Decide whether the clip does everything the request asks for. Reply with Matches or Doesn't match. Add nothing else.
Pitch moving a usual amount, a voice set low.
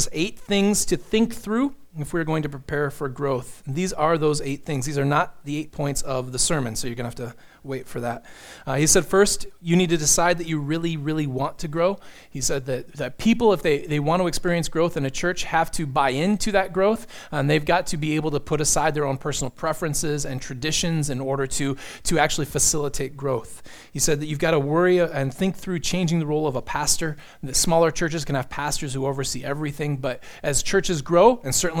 Doesn't match